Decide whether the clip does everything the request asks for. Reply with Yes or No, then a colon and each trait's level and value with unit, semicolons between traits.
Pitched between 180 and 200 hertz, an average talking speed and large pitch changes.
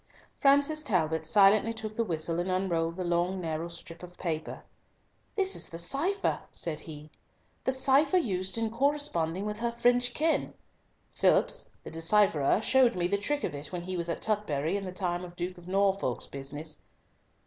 Yes: medium, 185 Hz; average, 180 wpm; wide, 5.8 semitones